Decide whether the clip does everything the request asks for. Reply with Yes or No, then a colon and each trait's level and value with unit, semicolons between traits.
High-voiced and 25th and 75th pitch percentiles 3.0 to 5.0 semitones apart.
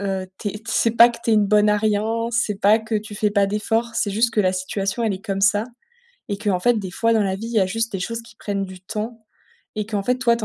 No: high, 210 Hz; narrow, 2.4 semitones